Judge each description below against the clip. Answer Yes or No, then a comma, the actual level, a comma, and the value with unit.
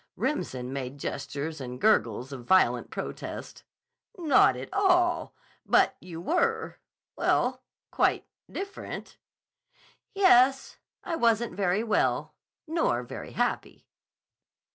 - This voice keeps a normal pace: No, slow, 100 wpm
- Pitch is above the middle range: Yes, high, 225 Hz